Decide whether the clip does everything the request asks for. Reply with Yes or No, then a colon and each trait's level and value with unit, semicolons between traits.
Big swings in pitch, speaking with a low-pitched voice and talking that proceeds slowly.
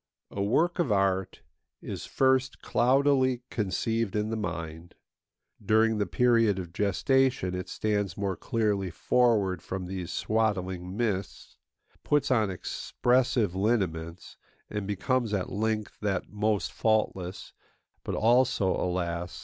No: average, 4.0 semitones; low, 105 Hz; slow, 120 wpm